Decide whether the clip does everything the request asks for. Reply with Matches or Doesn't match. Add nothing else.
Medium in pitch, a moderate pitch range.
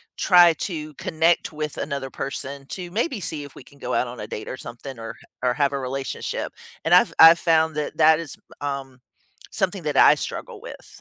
Matches